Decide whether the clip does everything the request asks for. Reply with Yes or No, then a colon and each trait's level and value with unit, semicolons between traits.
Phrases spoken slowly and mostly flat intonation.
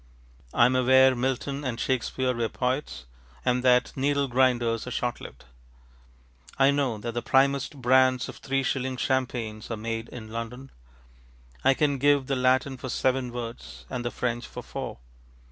No: average, 160 wpm; narrow, 1.8 semitones